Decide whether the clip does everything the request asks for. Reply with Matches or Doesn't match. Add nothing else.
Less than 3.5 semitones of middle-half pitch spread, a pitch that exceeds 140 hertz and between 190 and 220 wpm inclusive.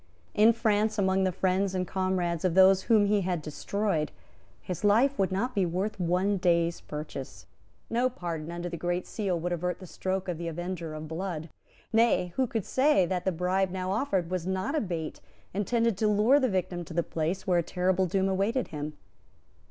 Matches